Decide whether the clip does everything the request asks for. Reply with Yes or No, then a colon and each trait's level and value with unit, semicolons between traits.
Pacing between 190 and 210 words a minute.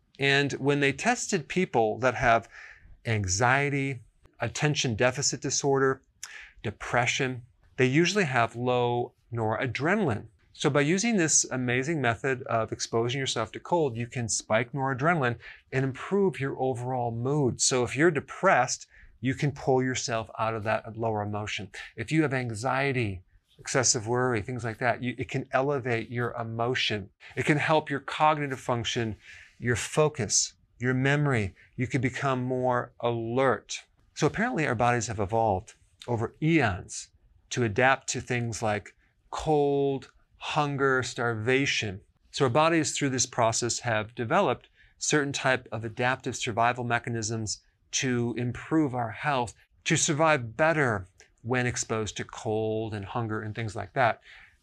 No: average, 140 wpm